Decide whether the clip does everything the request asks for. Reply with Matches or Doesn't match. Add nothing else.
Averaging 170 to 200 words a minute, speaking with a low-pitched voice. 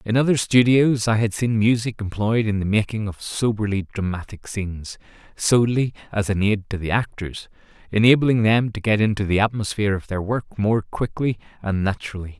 Matches